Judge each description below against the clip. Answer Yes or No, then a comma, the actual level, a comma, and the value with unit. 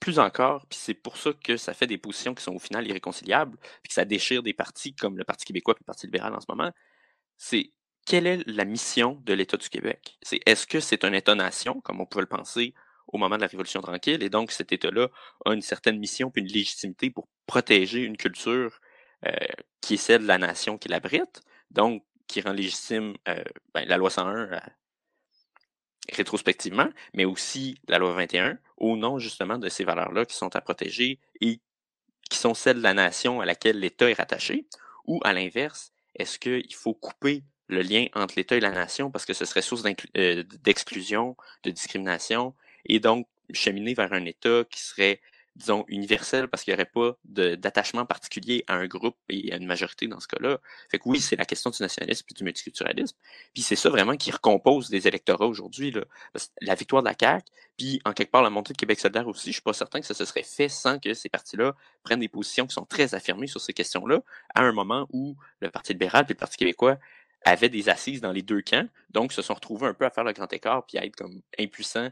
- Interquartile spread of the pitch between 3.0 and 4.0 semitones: No, average, 4.5 semitones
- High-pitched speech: No, low, 115 Hz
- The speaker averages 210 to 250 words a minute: Yes, fast, 220 wpm